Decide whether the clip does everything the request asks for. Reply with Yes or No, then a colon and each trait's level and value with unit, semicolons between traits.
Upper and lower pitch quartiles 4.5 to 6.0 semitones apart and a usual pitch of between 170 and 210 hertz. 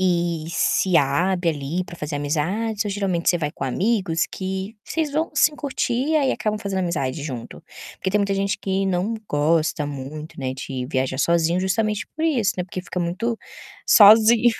Yes: average, 5.3 semitones; medium, 185 Hz